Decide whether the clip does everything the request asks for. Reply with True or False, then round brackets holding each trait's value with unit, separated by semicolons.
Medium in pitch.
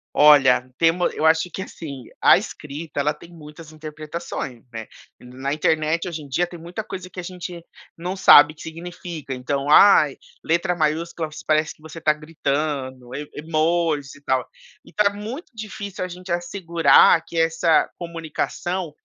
True (160 Hz)